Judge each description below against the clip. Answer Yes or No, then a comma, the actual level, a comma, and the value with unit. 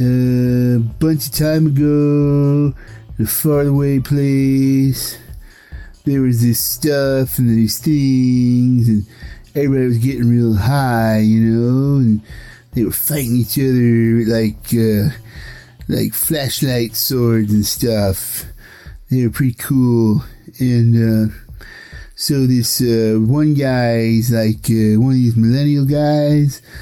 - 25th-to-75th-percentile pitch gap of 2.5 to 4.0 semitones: Yes, average, 3.5 semitones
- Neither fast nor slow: No, slow, 130 wpm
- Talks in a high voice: No, low, 125 Hz